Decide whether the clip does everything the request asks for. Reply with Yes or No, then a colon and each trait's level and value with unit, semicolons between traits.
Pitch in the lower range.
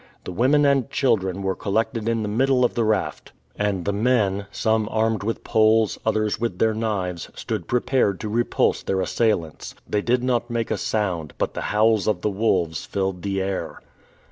Yes: low, 110 Hz